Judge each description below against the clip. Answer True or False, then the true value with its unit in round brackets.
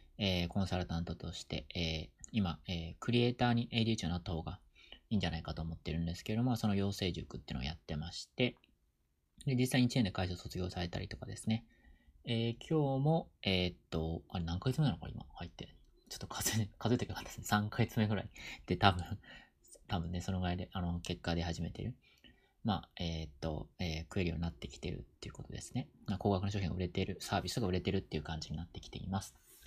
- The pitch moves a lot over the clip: False (4.7 semitones)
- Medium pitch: False (90 Hz)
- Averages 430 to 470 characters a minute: True (445 characters per minute)